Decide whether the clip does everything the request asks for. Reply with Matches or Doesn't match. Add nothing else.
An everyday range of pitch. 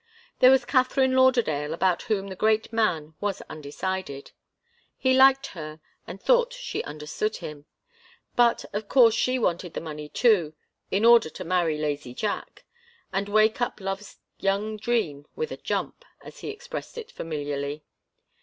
Doesn't match